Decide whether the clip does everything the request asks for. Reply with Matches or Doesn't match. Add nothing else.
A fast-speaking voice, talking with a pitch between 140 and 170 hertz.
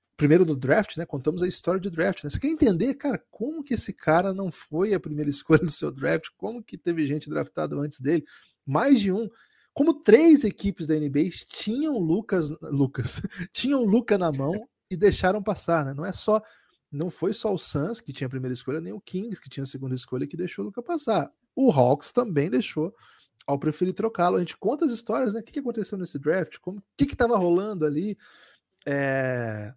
Doesn't match